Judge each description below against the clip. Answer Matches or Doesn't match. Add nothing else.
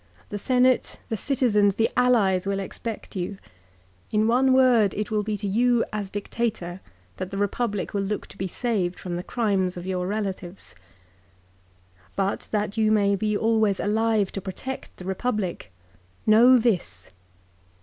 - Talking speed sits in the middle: Matches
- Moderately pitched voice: Doesn't match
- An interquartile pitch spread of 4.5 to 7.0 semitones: Doesn't match